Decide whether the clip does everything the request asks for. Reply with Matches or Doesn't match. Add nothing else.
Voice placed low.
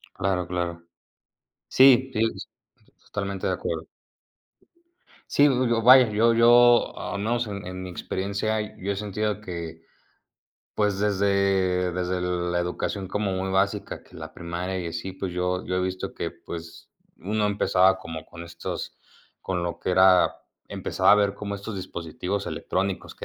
Matches